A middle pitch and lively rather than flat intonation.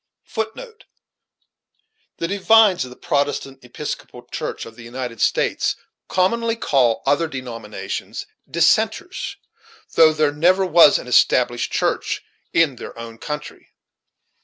Yes: medium, 150 Hz; wide, 6.9 semitones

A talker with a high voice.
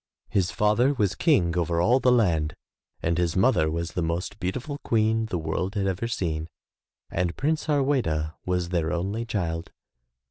No: very low, 90 Hz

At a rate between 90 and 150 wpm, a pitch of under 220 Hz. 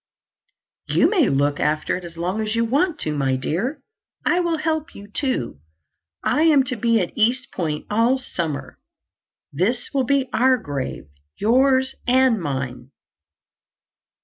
No: average, 145 wpm; high, 225 Hz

